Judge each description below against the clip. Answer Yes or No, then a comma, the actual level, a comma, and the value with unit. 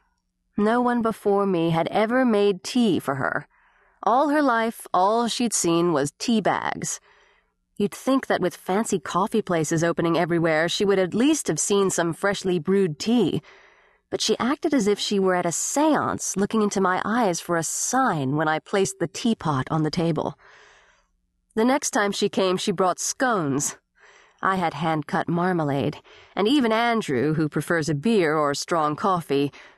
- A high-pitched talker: Yes, high, 195 Hz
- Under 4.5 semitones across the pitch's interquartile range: No, average, 5.2 semitones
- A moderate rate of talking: Yes, average, 175 wpm